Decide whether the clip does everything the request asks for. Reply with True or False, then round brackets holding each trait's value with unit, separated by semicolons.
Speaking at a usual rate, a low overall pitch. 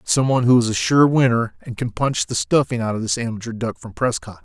False (255 wpm; 120 Hz)